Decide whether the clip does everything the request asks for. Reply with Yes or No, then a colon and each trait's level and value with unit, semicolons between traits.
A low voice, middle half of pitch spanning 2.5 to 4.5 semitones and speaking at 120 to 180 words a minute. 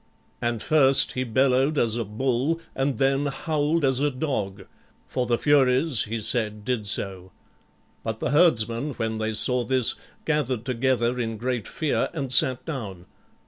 Yes: low, 125 Hz; average, 3.5 semitones; average, 155 wpm